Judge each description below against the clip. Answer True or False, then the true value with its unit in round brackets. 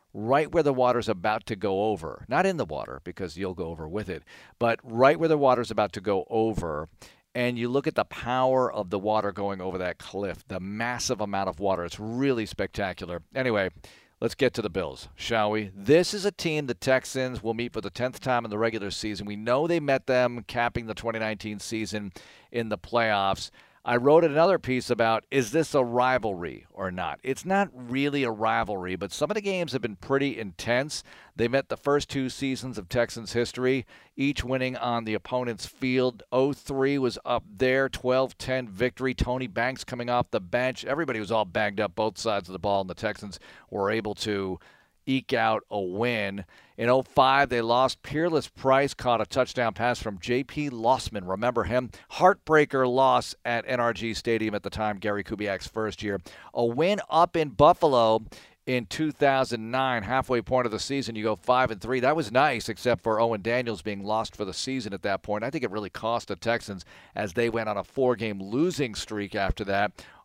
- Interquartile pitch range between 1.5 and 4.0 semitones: True (3.7 semitones)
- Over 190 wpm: True (200 wpm)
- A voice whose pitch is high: False (120 Hz)